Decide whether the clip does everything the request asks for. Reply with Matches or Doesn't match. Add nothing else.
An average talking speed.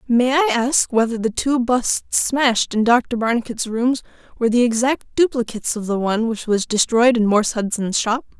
Matches